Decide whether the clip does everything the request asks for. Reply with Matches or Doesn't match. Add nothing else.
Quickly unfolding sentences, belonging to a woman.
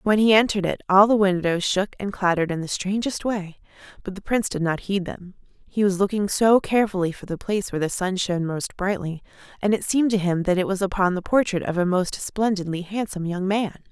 Matches